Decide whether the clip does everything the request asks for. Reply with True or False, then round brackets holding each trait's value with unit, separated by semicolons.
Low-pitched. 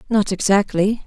False (205 Hz)